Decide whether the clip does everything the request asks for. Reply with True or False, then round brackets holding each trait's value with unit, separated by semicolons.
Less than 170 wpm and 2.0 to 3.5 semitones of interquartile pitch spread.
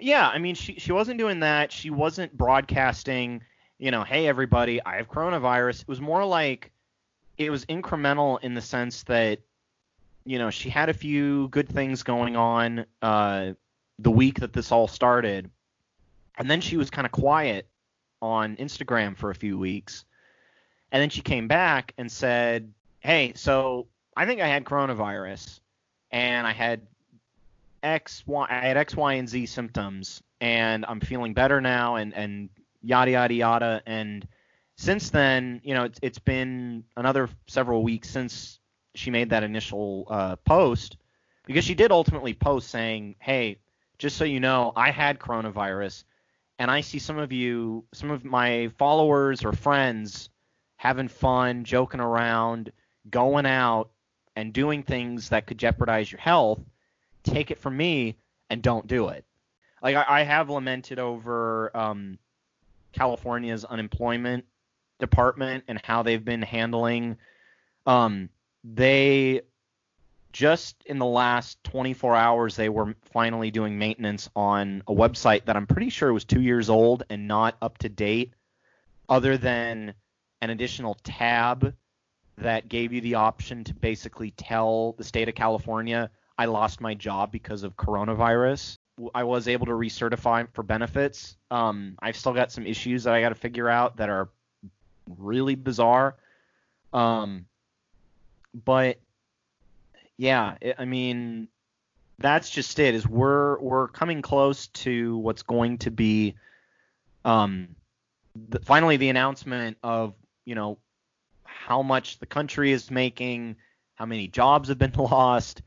True (150 wpm; 2.8 semitones)